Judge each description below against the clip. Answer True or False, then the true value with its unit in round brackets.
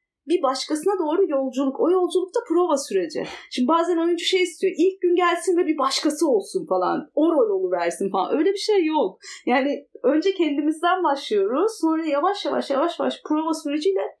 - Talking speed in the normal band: False (170 wpm)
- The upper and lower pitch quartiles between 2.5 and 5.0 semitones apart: True (4.3 semitones)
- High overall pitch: True (330 Hz)